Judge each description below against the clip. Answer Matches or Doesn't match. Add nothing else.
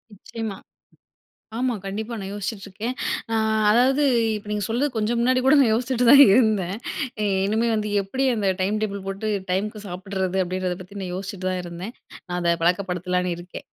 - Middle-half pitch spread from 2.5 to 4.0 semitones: Matches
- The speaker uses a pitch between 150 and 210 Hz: Matches